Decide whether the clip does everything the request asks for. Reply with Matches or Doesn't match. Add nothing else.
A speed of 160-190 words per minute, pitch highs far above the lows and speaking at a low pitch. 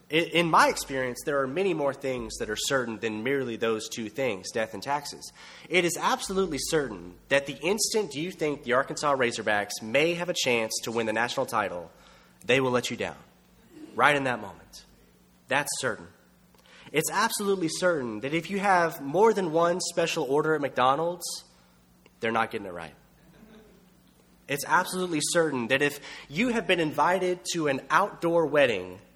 Doesn't match